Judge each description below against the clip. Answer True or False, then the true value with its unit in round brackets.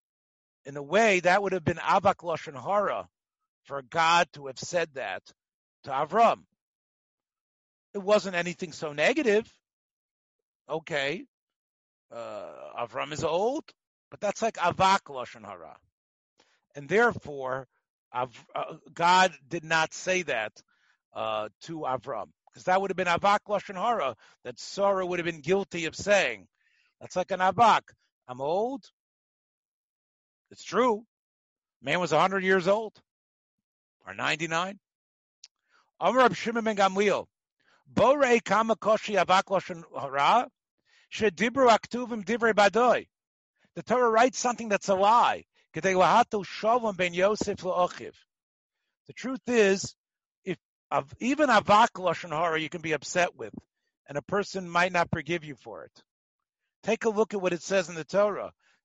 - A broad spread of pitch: False (4.5 semitones)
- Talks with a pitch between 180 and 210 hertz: True (190 Hz)